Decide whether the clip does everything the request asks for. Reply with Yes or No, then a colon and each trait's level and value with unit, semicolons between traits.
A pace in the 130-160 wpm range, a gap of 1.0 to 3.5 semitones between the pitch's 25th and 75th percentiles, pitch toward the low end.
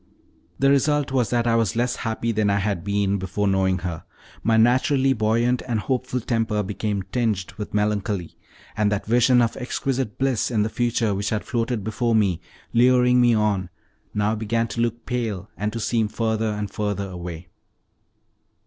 No: average, 175 wpm; average, 2.8 semitones; low, 110 Hz